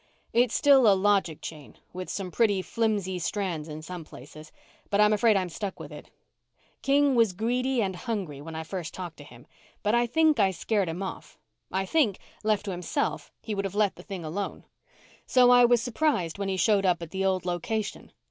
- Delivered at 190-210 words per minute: Yes, fast, 205 wpm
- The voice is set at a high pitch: Yes, high, 195 Hz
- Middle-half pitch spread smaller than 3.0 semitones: No, average, 4.3 semitones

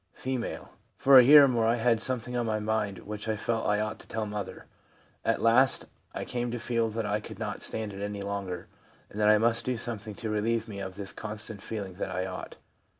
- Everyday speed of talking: No, fast, 230 wpm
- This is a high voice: No, low, 110 Hz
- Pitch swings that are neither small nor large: No, narrow, 2.2 semitones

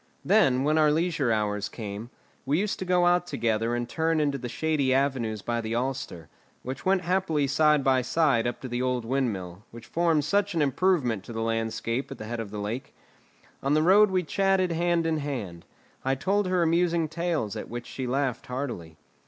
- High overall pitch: No, low, 135 Hz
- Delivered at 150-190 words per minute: No, average, 200 wpm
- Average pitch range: No, wide, 6.1 semitones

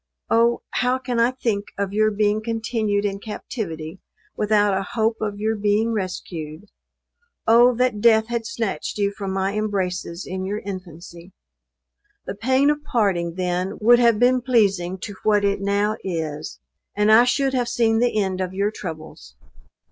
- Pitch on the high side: Yes, high, 210 Hz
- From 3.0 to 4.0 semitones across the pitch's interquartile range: Yes, average, 3.3 semitones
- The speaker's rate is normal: Yes, average, 165 wpm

